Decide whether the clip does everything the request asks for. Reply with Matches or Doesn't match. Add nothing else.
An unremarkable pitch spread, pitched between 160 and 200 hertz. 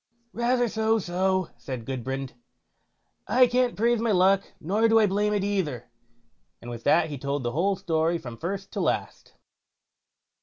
Doesn't match